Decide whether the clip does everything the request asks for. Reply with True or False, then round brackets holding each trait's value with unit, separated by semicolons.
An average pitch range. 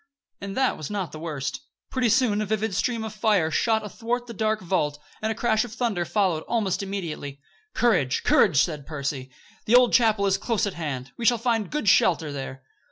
False (6.2 semitones)